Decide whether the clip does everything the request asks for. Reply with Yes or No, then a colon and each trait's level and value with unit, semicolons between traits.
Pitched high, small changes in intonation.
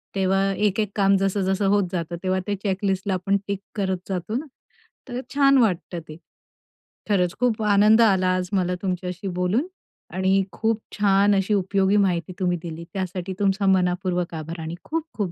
Yes: high, 195 Hz; narrow, 2.0 semitones